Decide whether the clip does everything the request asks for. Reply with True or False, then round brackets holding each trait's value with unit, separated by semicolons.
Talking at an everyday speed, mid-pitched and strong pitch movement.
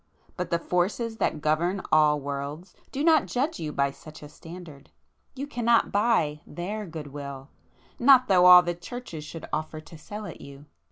True (170 wpm; 170 Hz; 6.0 semitones)